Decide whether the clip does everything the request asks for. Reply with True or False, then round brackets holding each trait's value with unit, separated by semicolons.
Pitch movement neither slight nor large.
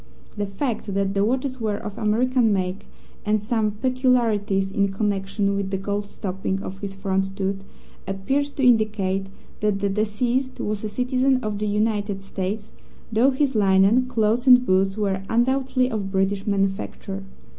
True (3.5 semitones)